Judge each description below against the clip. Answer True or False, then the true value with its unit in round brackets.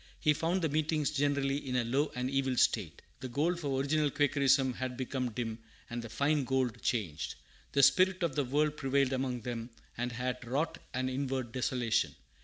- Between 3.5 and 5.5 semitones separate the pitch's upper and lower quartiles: False (2.7 semitones)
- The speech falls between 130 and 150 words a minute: False (185 wpm)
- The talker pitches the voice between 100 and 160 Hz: True (135 Hz)